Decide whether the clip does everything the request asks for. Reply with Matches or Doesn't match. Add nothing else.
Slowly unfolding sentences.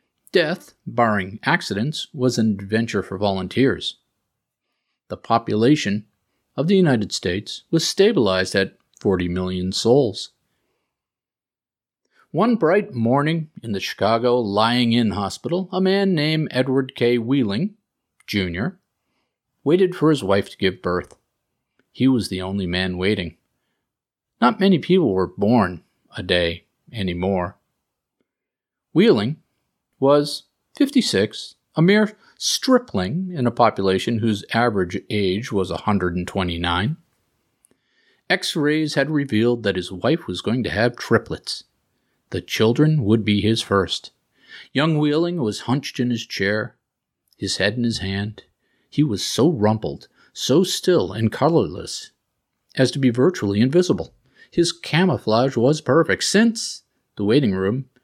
Matches